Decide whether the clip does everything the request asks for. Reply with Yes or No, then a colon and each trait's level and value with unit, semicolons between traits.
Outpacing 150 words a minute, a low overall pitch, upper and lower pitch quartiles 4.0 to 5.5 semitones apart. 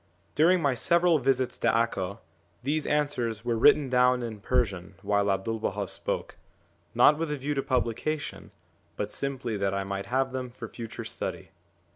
Yes: average, 165 wpm; low, 125 Hz; average, 4.9 semitones